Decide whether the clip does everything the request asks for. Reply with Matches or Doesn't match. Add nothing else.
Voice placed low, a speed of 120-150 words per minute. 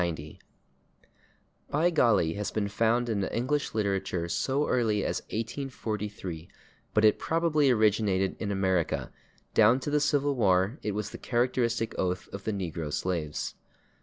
Matches